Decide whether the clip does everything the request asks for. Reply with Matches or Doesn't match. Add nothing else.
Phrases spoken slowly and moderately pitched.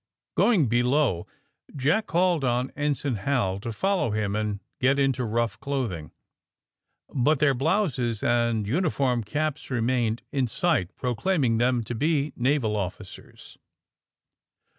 Doesn't match